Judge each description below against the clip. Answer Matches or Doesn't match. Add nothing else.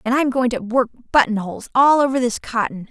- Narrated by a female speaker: Matches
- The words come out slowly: Doesn't match